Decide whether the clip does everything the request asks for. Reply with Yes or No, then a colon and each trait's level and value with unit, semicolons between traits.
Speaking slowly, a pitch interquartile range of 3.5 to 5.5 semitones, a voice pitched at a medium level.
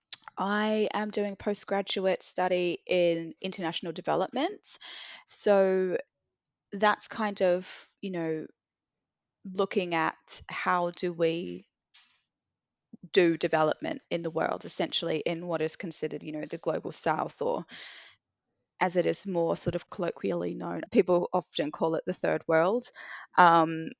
No: slow, 130 wpm; average, 3.1 semitones; medium, 180 Hz